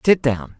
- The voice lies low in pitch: Yes, low, 130 Hz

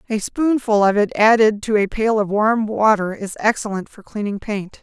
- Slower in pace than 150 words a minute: No, average, 200 wpm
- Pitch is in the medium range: No, high, 210 Hz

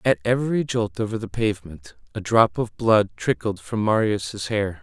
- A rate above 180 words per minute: No, average, 175 wpm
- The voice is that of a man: Yes, male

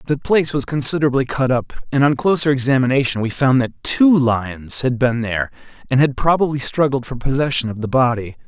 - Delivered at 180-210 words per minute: Yes, average, 190 wpm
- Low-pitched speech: Yes, low, 130 Hz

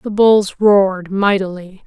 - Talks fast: No, slow, 130 wpm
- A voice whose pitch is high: Yes, high, 195 Hz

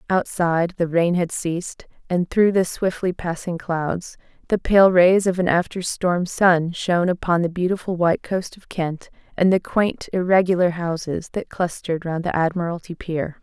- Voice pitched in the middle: Yes, medium, 175 Hz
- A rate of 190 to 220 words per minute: No, average, 170 wpm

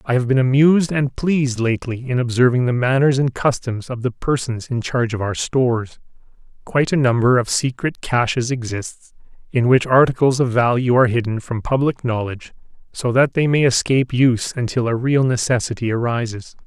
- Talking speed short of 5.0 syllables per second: No, 5.5 syllables/s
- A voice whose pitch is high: No, low, 125 Hz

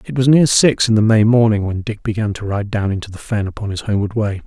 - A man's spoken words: Yes, male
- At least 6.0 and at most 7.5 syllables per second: Yes, 6.2 syllables/s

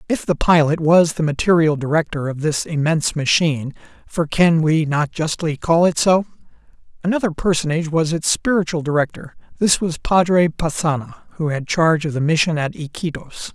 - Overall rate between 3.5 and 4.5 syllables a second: No, 5.3 syllables/s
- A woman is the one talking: No, male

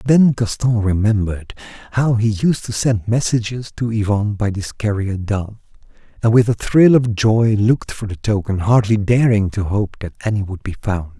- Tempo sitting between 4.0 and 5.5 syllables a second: Yes, 4.9 syllables/s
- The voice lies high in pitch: No, low, 110 Hz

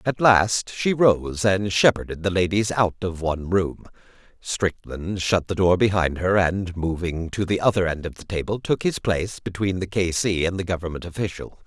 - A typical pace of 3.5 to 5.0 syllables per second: Yes, 4.9 syllables/s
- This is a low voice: Yes, very low, 95 Hz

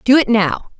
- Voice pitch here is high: Yes, high, 235 Hz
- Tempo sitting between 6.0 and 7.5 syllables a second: No, 4.6 syllables/s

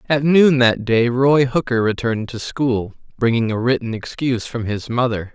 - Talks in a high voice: No, low, 120 Hz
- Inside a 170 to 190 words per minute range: Yes, average, 180 wpm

